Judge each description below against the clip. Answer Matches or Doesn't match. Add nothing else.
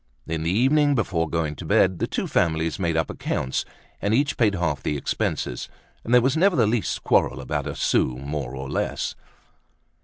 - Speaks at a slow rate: Doesn't match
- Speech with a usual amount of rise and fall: Doesn't match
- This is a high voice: Doesn't match